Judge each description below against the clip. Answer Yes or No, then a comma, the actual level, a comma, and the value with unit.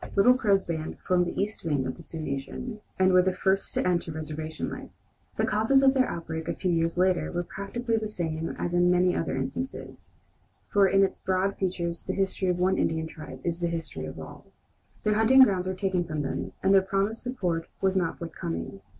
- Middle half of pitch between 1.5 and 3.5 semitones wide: Yes, average, 3.2 semitones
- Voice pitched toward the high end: No, medium, 180 Hz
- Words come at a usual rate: No, fast, 210 wpm